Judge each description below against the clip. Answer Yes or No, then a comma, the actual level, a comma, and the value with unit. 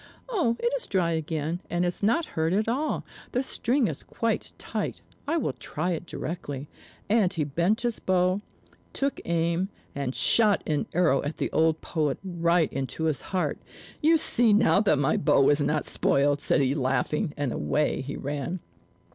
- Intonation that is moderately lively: No, wide, 6.3 semitones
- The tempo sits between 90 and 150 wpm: No, average, 175 wpm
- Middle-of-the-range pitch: Yes, medium, 170 Hz